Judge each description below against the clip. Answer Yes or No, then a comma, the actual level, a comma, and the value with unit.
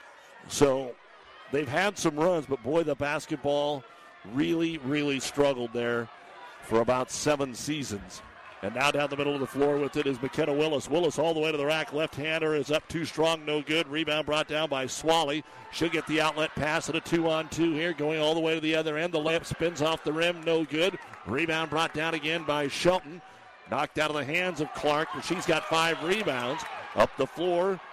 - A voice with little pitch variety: Yes, narrow, 2.1 semitones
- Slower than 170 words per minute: No, fast, 205 wpm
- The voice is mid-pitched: Yes, medium, 155 Hz